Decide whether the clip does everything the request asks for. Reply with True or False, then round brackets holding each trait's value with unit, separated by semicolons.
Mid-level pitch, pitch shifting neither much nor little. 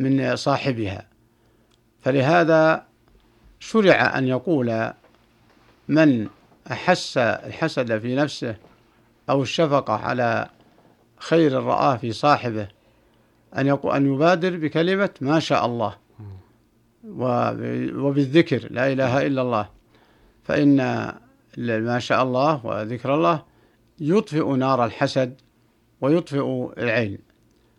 False (130 Hz; 4.4 semitones)